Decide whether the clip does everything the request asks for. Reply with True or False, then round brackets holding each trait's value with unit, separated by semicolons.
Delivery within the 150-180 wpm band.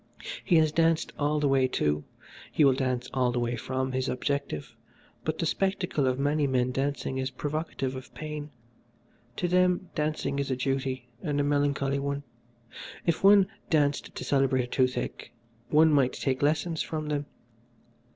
True (165 wpm)